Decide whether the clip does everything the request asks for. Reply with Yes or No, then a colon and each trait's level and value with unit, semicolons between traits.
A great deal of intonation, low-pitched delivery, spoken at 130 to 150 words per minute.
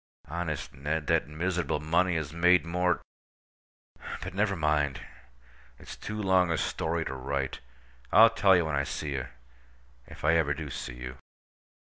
No: average, 4.3 semitones; very low, 80 Hz; average, 145 wpm